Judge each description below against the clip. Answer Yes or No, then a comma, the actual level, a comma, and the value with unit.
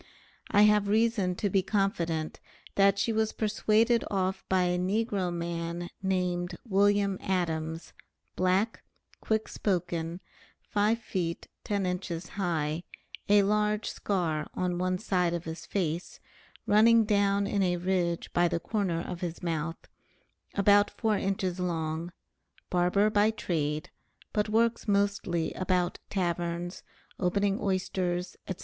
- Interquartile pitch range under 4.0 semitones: Yes, average, 2.9 semitones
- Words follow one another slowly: Yes, slow, 130 wpm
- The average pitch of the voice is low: No, medium, 185 Hz